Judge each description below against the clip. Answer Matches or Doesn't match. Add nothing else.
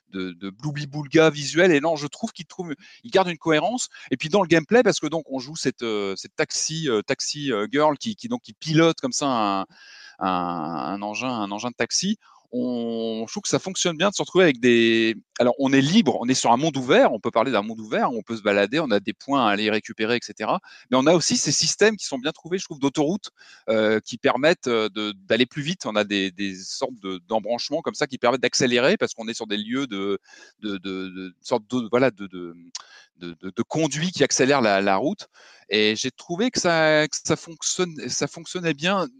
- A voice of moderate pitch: Doesn't match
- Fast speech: Doesn't match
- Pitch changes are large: Matches